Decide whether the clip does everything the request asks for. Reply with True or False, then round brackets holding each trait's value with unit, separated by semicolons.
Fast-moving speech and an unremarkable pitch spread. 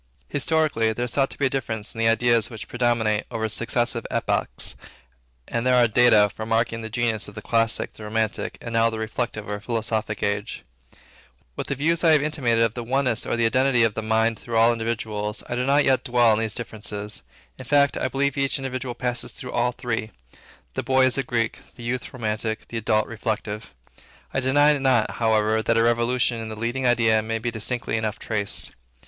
False (210 wpm; 2.2 semitones)